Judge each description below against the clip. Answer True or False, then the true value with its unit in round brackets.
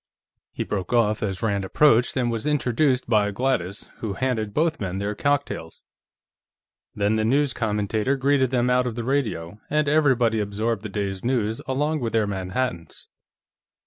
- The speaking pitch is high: False (115 Hz)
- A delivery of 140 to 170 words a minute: True (160 wpm)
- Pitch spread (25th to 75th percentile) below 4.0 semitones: False (4.3 semitones)